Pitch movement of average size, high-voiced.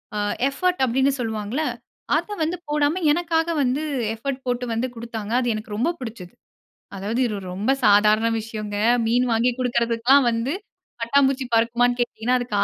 Yes: average, 3.4 semitones; high, 240 Hz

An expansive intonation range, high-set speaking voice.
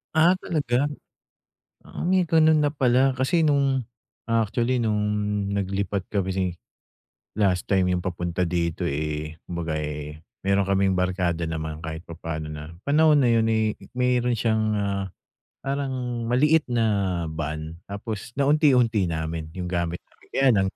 No: wide, 6.9 semitones; low, 100 Hz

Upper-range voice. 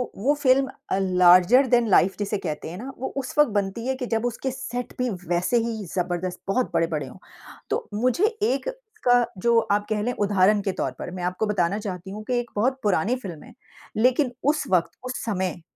Yes: high, 210 Hz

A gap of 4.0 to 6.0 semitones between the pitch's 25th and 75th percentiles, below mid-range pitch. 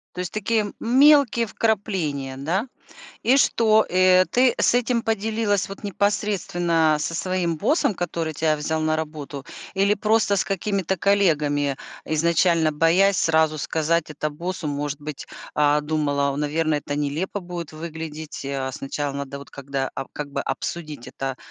No: average, 5.1 semitones; medium, 165 Hz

